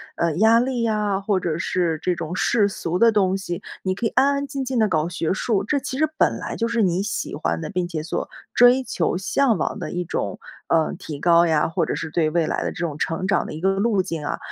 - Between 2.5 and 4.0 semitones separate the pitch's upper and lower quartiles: No, average, 5.3 semitones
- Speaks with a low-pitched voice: No, medium, 185 Hz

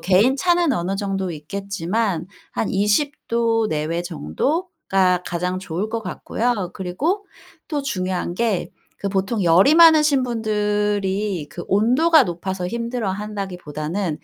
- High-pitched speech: Yes, high, 200 Hz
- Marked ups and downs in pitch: No, average, 4.6 semitones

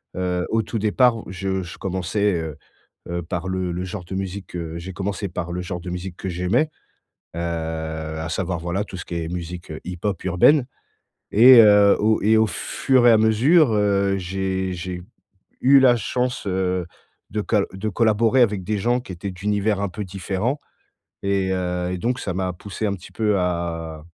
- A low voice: Yes, very low, 95 Hz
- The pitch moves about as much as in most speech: Yes, average, 3.1 semitones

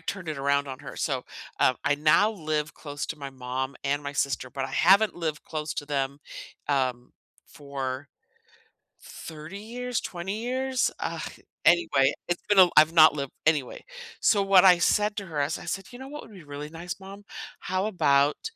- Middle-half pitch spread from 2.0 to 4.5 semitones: No, wide, 5.5 semitones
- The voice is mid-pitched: Yes, medium, 155 Hz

